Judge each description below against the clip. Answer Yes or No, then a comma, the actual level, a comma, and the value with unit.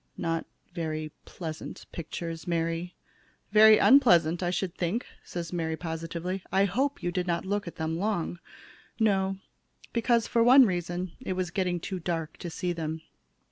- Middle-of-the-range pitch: Yes, medium, 175 Hz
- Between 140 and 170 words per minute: Yes, average, 150 wpm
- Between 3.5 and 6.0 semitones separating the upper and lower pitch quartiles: No, average, 2.8 semitones